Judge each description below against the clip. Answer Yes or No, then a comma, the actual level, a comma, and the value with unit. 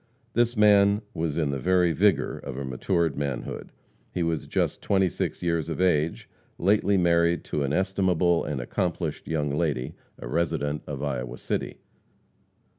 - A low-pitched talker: Yes, very low, 85 Hz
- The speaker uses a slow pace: No, average, 155 wpm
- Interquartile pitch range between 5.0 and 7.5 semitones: No, average, 4.2 semitones